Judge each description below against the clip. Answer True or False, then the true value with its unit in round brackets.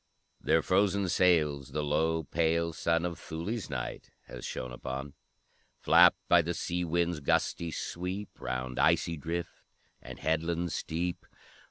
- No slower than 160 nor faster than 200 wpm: False (135 wpm)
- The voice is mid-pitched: False (85 Hz)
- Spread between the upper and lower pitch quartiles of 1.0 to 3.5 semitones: True (2.5 semitones)